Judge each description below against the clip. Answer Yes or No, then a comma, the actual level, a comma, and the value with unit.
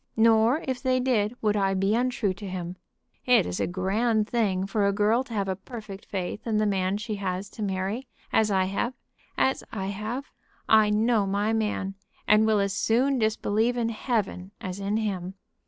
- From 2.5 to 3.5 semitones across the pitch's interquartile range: Yes, average, 2.8 semitones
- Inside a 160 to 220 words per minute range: Yes, average, 190 wpm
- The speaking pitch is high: Yes, high, 210 Hz